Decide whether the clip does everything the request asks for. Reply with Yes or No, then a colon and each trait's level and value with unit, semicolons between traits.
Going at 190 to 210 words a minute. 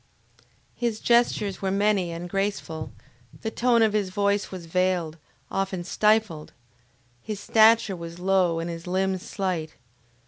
No: slow, 135 wpm